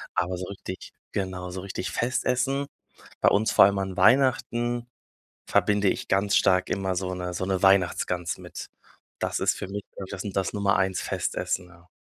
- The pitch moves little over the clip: Yes, narrow, 2.0 semitones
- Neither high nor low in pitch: No, very low, 95 Hz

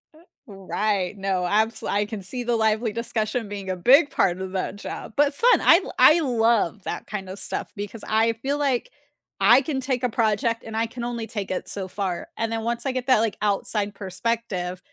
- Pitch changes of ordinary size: Yes, average, 3.3 semitones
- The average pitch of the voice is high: Yes, high, 220 Hz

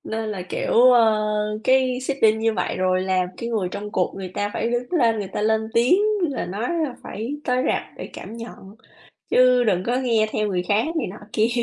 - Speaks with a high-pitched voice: Yes, high, 225 Hz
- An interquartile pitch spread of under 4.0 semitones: Yes, average, 3.4 semitones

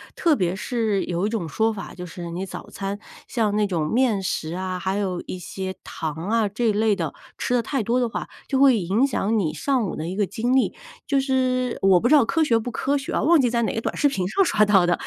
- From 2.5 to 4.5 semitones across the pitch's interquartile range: No, average, 4.9 semitones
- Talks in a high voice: Yes, high, 215 Hz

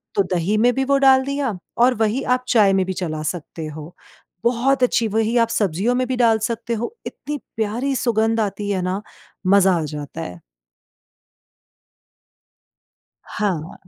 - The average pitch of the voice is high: Yes, high, 220 Hz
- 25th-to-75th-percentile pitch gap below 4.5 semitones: No, average, 4.8 semitones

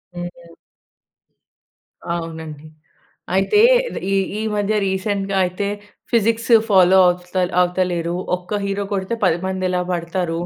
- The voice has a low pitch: No, medium, 185 Hz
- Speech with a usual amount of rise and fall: No, narrow, 2.2 semitones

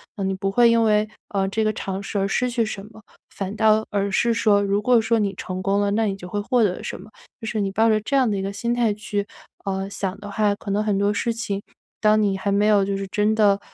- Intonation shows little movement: Yes, narrow, 1.8 semitones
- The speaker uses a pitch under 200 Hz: No, high, 205 Hz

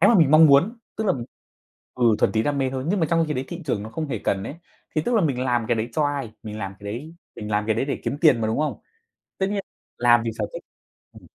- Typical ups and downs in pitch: No, wide, 5.8 semitones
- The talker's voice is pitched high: No, low, 135 Hz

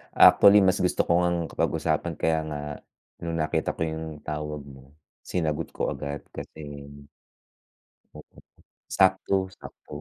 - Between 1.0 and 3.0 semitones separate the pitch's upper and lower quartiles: Yes, average, 2.7 semitones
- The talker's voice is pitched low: Yes, very low, 80 Hz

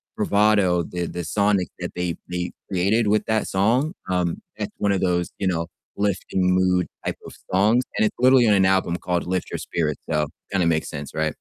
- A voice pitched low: Yes, very low, 95 Hz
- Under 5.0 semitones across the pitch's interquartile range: Yes, average, 2.7 semitones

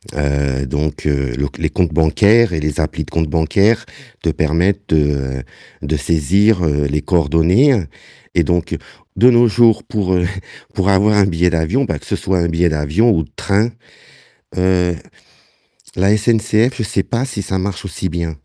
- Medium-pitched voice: No, very low, 90 Hz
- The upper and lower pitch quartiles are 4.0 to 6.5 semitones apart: Yes, average, 4.9 semitones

